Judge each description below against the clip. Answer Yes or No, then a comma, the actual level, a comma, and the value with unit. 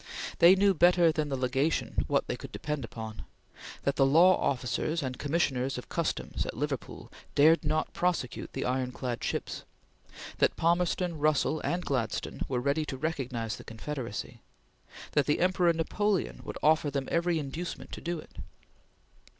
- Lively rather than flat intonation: No, average, 4.4 semitones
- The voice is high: No, medium, 150 Hz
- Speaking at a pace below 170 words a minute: Yes, average, 155 wpm